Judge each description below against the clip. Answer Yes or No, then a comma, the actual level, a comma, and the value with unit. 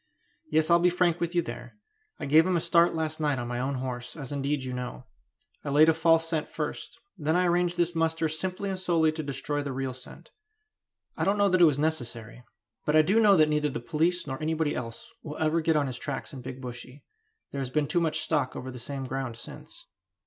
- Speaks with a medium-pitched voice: Yes, medium, 155 Hz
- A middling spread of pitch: Yes, average, 4.0 semitones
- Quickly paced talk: Yes, fast, 235 wpm